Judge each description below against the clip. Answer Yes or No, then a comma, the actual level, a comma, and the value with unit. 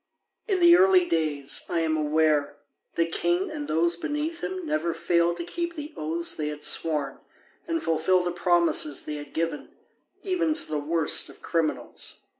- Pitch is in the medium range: Yes, medium, 170 Hz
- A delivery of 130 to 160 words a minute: No, average, 170 wpm